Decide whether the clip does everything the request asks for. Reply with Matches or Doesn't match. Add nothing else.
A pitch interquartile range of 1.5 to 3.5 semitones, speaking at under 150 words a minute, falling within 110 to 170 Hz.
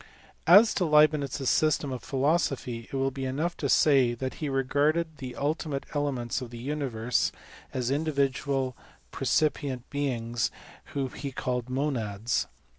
Matches